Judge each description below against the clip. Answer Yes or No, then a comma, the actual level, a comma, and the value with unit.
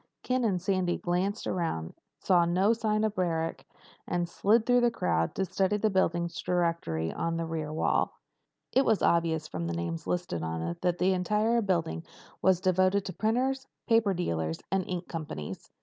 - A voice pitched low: No, medium, 180 Hz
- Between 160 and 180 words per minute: Yes, average, 175 wpm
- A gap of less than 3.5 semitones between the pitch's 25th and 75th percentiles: No, average, 4.0 semitones